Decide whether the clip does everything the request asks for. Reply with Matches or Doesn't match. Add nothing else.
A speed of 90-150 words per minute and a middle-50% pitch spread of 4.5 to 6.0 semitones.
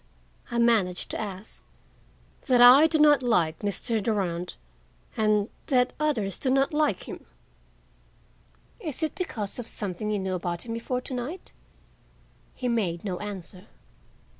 Matches